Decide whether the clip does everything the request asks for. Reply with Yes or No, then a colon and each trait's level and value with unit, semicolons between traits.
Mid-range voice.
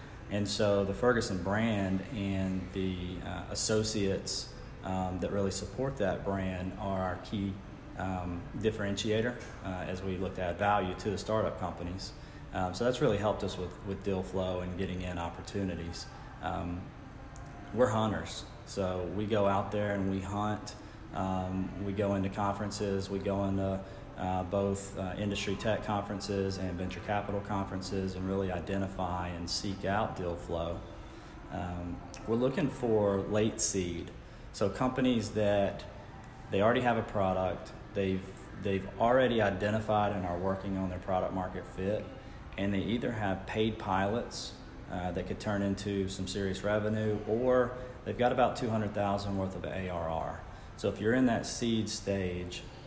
No: low, 100 Hz